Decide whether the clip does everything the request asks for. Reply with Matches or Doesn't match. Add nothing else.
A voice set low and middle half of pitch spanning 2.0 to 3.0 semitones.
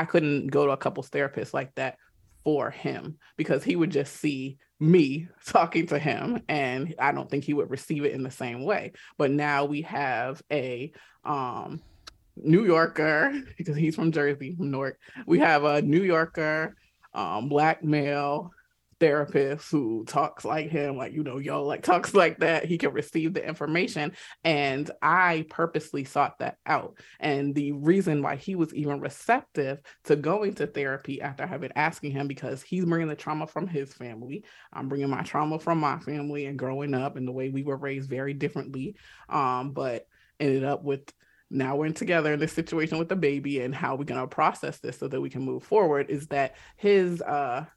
Doesn't match